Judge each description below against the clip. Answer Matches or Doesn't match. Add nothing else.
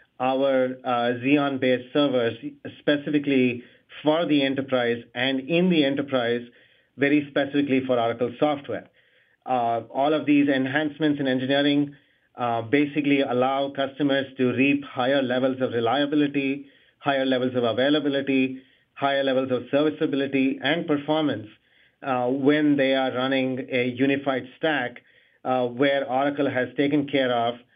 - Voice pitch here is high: Doesn't match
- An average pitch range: Doesn't match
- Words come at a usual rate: Doesn't match